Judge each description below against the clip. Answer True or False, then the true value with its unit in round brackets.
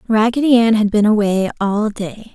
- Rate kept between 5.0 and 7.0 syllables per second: False (4.8 syllables/s)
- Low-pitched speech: False (215 Hz)